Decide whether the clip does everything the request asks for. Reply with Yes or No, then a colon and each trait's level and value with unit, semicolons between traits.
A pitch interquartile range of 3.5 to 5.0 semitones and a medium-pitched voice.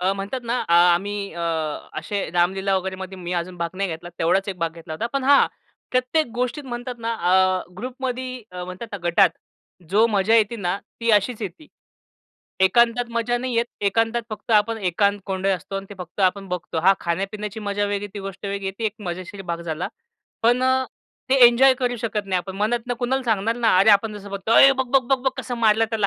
No: average, 4.0 semitones; high, 205 Hz